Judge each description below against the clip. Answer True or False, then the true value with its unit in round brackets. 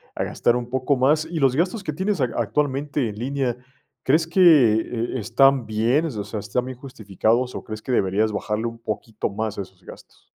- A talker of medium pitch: False (125 Hz)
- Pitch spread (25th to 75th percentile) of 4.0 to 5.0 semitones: True (4.5 semitones)